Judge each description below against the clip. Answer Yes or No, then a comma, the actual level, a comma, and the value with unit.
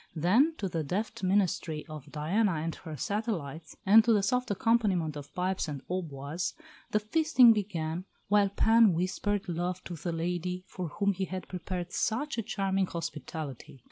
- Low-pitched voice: No, medium, 185 Hz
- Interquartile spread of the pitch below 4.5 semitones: Yes, average, 4.1 semitones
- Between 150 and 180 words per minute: Yes, average, 165 wpm